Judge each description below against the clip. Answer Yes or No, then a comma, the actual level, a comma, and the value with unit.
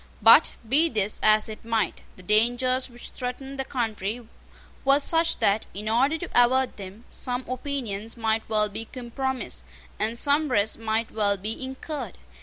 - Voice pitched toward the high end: Yes, high, 235 Hz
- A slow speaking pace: No, average, 160 wpm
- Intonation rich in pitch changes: No, average, 3.5 semitones